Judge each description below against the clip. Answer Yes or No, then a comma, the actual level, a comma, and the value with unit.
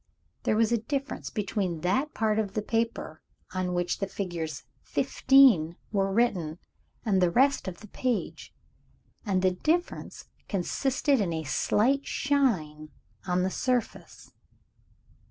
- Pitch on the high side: Yes, high, 205 Hz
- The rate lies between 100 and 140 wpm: Yes, slow, 135 wpm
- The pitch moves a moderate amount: No, wide, 5.7 semitones